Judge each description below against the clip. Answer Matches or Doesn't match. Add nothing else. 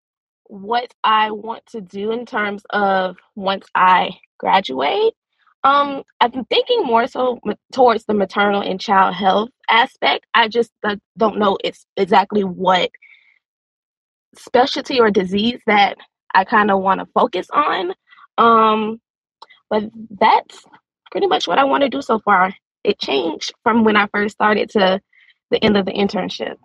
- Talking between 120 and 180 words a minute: Matches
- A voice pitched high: Matches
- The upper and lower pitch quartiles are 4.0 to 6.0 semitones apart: Doesn't match